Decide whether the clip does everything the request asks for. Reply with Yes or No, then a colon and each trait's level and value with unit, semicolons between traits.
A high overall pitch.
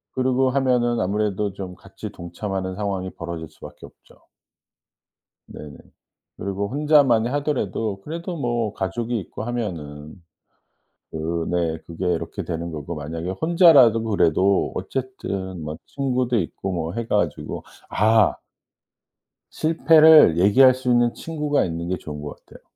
No: low, 105 Hz